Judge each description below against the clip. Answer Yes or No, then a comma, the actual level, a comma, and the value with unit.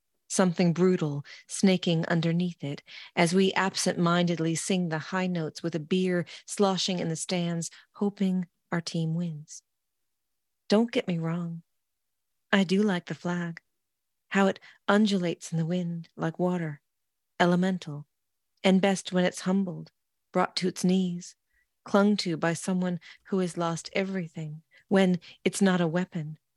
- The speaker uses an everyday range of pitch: No, narrow, 2.3 semitones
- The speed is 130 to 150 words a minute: Yes, average, 140 wpm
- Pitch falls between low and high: Yes, medium, 175 Hz